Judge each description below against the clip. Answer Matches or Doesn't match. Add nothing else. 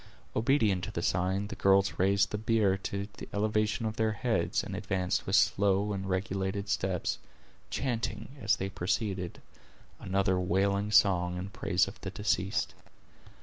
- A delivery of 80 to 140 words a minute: Doesn't match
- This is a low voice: Matches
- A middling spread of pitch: Doesn't match